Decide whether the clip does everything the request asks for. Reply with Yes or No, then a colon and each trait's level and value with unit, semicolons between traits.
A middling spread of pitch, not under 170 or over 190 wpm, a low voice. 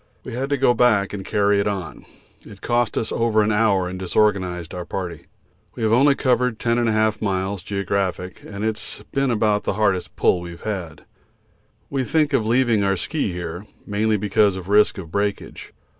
Yes: average, 3.3 semitones; average, 185 wpm; low, 105 Hz